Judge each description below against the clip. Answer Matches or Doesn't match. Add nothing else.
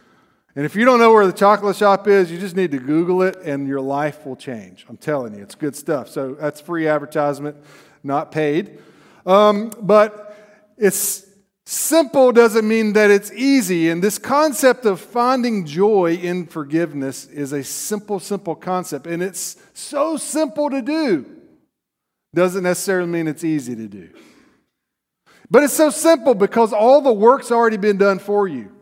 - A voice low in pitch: Doesn't match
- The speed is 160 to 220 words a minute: Matches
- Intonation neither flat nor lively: Doesn't match